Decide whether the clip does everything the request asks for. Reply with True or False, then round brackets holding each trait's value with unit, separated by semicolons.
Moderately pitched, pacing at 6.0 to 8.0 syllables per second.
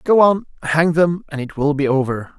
False (155 Hz; 5.0 syllables/s)